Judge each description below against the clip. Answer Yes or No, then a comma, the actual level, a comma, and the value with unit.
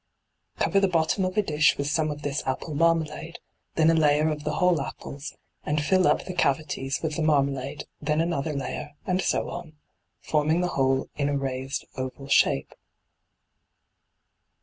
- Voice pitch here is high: No, medium, 150 Hz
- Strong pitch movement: No, average, 2.8 semitones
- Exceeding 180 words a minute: No, average, 170 wpm